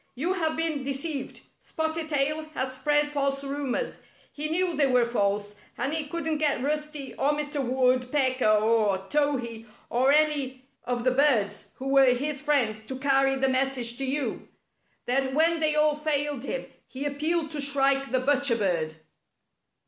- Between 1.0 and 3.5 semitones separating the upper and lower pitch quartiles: Yes, average, 2.8 semitones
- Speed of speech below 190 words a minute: Yes, average, 165 wpm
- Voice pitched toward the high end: Yes, very high, 275 Hz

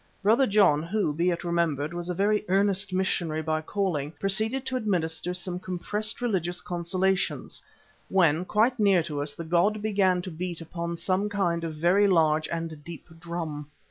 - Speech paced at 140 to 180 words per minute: Yes, average, 170 wpm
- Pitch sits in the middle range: Yes, medium, 175 Hz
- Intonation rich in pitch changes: No, average, 3.2 semitones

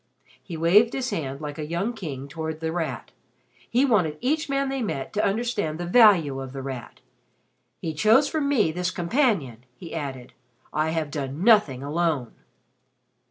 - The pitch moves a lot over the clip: Yes, wide, 7.2 semitones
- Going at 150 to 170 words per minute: Yes, average, 165 wpm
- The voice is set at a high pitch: No, medium, 165 Hz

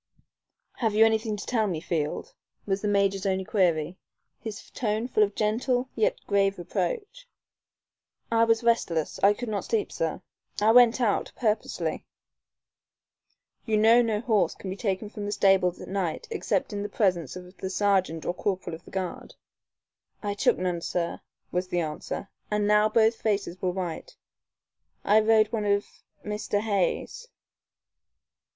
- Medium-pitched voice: No, high, 205 Hz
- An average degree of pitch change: Yes, average, 3.1 semitones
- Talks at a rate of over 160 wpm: No, average, 155 wpm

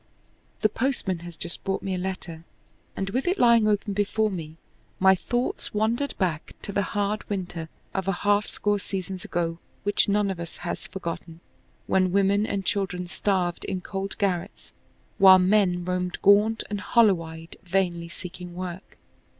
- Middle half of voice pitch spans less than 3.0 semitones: Yes, narrow, 2.6 semitones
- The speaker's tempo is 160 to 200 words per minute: Yes, average, 165 wpm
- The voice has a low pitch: No, high, 190 Hz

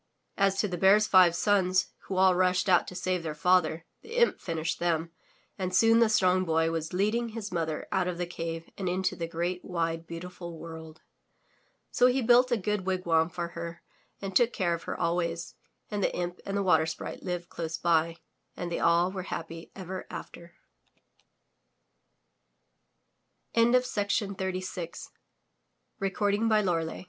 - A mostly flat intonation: Yes, narrow, 2.3 semitones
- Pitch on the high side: No, medium, 180 Hz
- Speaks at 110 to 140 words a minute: No, average, 155 wpm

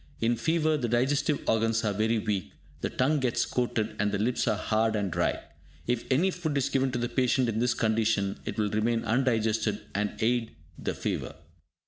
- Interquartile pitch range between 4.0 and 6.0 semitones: No, average, 2.8 semitones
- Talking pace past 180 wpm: Yes, average, 190 wpm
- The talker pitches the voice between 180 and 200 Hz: No, low, 115 Hz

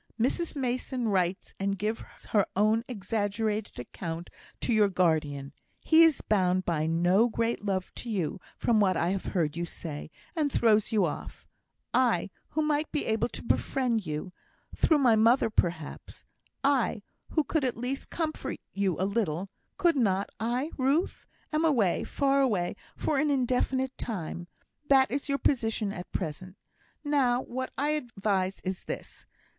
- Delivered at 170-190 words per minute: No, average, 155 wpm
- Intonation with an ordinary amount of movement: No, wide, 6.0 semitones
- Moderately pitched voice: No, high, 220 Hz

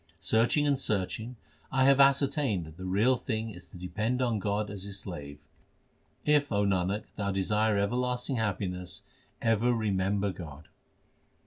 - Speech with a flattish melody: No, average, 4.6 semitones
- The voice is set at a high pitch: No, low, 105 Hz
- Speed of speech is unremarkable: Yes, average, 145 wpm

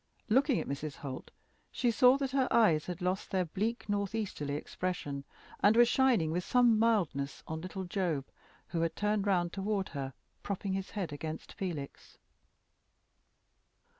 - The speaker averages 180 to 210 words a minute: No, average, 155 wpm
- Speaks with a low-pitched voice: No, high, 190 Hz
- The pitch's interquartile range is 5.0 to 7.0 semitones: Yes, wide, 5.5 semitones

